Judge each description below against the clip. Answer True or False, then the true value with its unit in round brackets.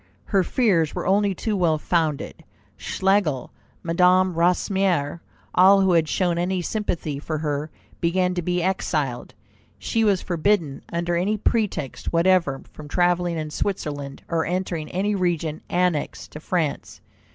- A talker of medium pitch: True (175 Hz)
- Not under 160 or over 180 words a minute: False (140 wpm)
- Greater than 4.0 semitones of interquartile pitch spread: False (3.2 semitones)